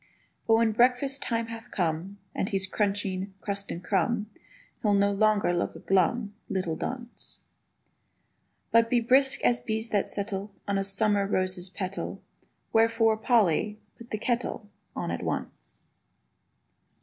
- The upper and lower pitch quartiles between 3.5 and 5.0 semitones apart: No, average, 2.8 semitones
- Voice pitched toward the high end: Yes, high, 205 Hz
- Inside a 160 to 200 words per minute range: No, average, 140 wpm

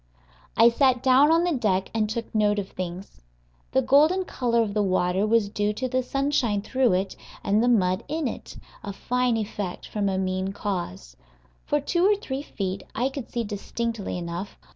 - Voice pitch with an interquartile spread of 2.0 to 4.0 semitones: No, average, 4.9 semitones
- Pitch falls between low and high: No, high, 220 Hz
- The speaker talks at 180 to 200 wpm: Yes, average, 185 wpm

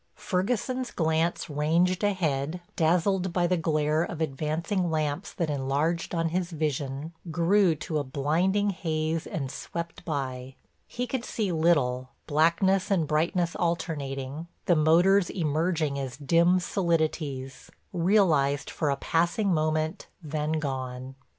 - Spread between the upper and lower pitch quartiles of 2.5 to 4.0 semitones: Yes, average, 3.3 semitones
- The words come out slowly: Yes, slow, 125 wpm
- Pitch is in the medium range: Yes, medium, 160 Hz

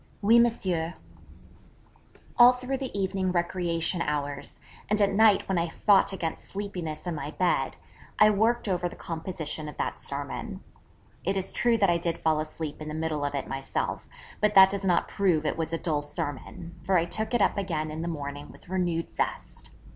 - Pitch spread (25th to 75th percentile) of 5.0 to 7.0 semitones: No, average, 4.2 semitones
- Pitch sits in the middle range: Yes, medium, 175 Hz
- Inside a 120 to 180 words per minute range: No, average, 190 wpm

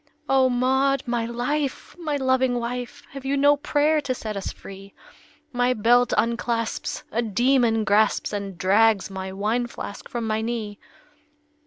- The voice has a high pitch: Yes, high, 240 Hz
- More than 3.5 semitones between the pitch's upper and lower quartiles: No, average, 3.2 semitones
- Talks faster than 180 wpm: No, average, 150 wpm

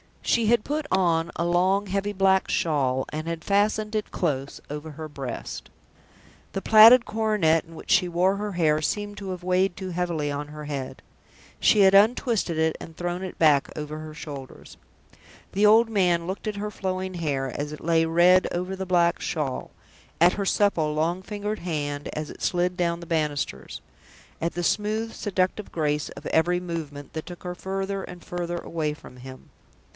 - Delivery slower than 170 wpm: No, average, 180 wpm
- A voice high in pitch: No, medium, 175 Hz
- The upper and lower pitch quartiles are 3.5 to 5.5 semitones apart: Yes, average, 4.0 semitones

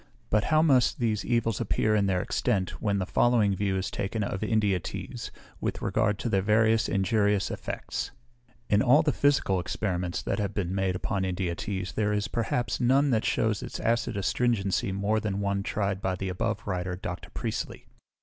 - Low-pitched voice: Yes, low, 100 Hz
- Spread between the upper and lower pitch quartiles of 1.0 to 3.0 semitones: Yes, narrow, 2.6 semitones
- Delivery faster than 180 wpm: Yes, average, 190 wpm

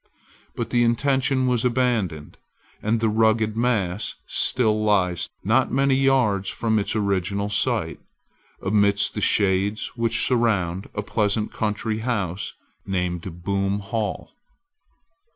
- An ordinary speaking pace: No, slow, 115 wpm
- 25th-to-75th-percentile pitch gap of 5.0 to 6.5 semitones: No, average, 3.0 semitones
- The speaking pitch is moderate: No, low, 105 Hz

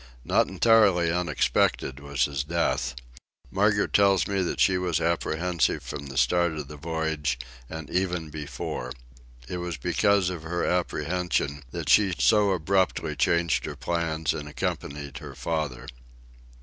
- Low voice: Yes, very low, 80 Hz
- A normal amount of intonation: Yes, average, 3.7 semitones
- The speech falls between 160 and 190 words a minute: No, slow, 135 wpm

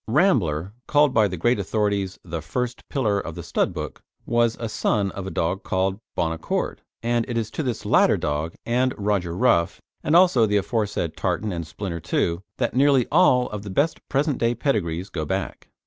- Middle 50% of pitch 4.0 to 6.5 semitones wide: Yes, wide, 5.5 semitones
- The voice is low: Yes, low, 105 Hz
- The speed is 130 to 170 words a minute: No, average, 195 wpm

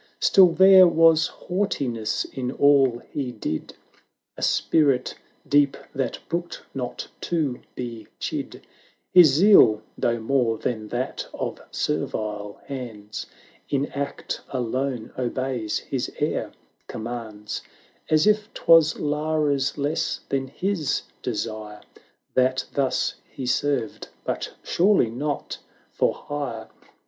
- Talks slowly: Yes, slow, 115 wpm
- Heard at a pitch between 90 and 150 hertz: Yes, low, 135 Hz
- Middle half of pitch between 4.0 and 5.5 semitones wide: Yes, average, 4.8 semitones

